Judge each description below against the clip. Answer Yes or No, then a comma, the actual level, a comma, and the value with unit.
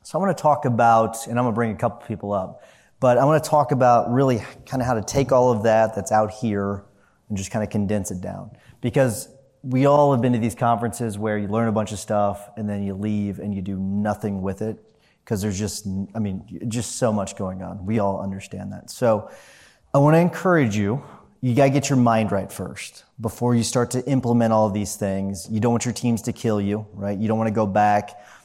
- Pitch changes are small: No, average, 3.3 semitones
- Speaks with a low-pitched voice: Yes, low, 110 Hz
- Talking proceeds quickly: Yes, fast, 250 wpm